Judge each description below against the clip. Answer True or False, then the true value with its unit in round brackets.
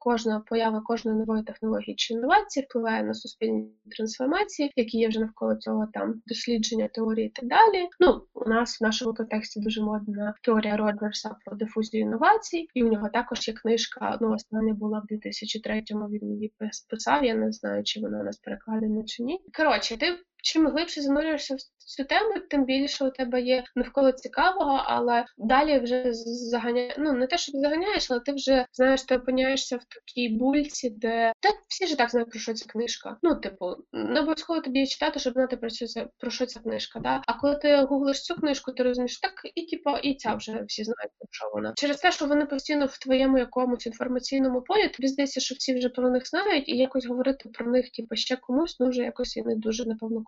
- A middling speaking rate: False (205 wpm)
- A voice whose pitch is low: False (245 Hz)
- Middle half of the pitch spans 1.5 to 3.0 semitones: False (3.9 semitones)